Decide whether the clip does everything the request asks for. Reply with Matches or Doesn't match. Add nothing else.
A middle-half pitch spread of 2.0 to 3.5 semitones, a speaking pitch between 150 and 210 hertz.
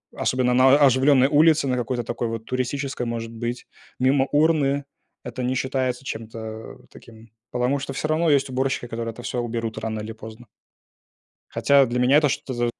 Doesn't match